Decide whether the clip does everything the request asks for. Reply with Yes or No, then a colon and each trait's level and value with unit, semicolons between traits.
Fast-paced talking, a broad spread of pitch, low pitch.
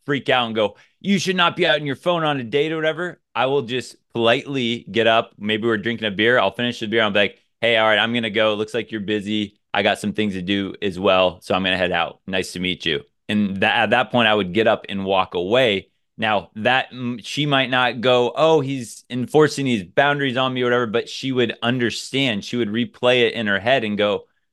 No: fast, 250 wpm; average, 3.8 semitones; low, 115 Hz